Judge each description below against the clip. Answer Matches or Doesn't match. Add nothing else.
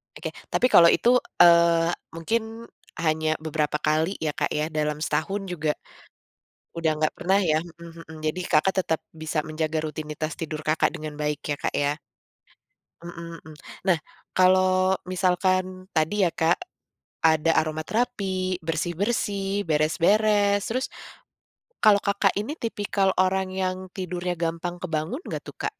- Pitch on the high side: Doesn't match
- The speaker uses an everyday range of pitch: Matches